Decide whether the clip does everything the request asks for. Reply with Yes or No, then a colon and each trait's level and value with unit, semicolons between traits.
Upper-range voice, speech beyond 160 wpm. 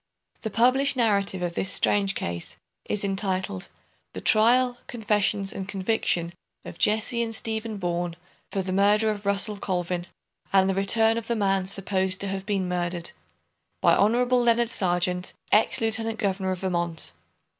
No: high, 200 Hz; average, 155 wpm